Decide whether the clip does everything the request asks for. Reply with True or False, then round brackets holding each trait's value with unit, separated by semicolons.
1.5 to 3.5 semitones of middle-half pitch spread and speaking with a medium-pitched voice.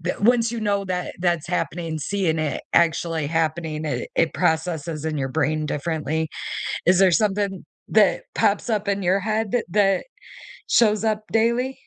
False (4.6 semitones; 180 Hz)